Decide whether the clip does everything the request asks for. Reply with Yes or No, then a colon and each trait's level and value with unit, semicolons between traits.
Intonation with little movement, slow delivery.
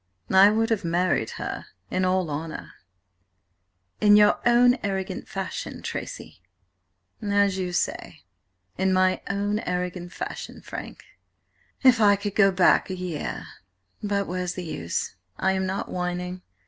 Yes: narrow, 2.2 semitones; slow, 130 wpm